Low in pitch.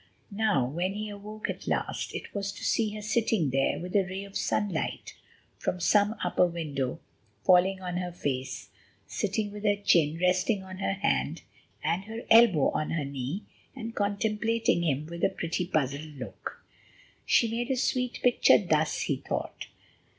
No: medium, 185 Hz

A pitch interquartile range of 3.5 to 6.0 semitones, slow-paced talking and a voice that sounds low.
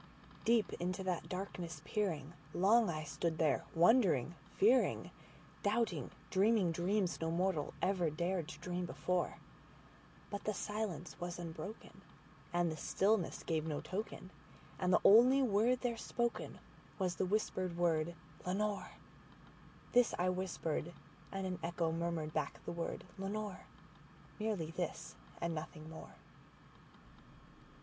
No: average, 3.8 semitones; slow, 115 wpm; medium, 180 Hz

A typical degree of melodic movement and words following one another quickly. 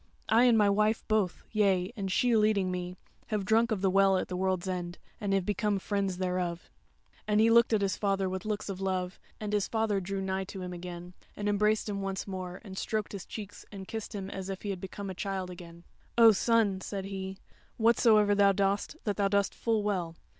No: narrow, 2.1 semitones; fast, 220 wpm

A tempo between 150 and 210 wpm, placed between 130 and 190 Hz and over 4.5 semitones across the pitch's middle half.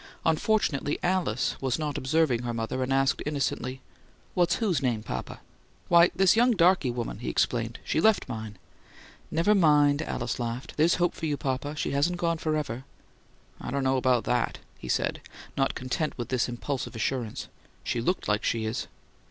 Yes: average, 170 wpm; medium, 140 Hz; average, 5.0 semitones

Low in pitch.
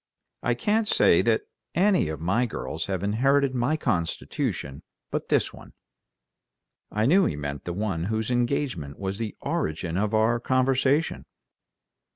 Yes: low, 110 Hz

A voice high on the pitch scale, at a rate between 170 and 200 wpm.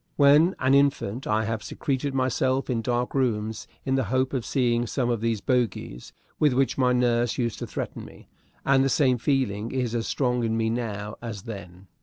No: low, 120 Hz; average, 195 wpm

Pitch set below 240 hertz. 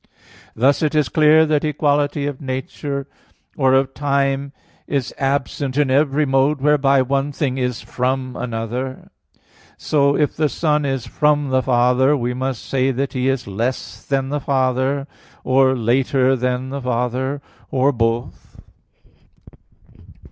Yes: low, 135 Hz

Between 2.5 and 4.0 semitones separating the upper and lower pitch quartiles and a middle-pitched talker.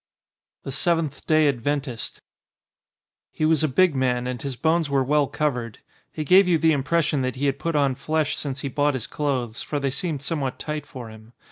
Yes: average, 3.1 semitones; medium, 145 Hz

